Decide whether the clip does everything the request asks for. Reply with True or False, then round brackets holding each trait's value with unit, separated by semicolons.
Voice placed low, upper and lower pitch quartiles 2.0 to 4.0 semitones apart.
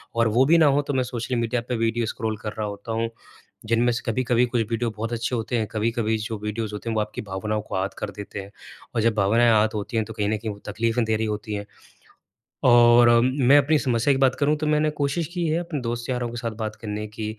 True (115 Hz; 2.4 semitones)